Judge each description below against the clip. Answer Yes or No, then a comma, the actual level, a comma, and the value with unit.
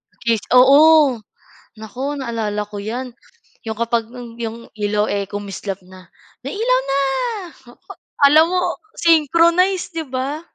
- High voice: Yes, very high, 255 Hz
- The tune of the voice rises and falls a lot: Yes, wide, 6.7 semitones